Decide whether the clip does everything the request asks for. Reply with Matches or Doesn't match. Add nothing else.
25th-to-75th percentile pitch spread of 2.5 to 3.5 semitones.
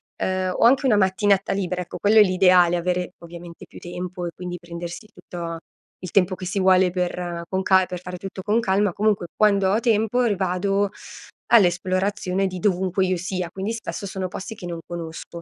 Doesn't match